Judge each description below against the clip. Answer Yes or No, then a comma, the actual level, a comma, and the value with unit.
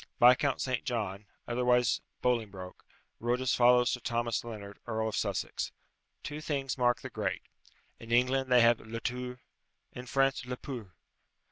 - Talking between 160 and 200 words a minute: No, average, 150 wpm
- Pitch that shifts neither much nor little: No, narrow, 1.6 semitones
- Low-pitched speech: Yes, low, 120 Hz